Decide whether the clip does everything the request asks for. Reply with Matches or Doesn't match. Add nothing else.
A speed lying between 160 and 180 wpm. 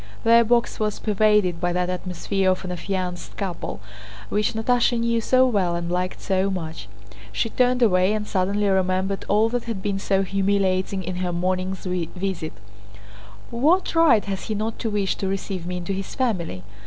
Matches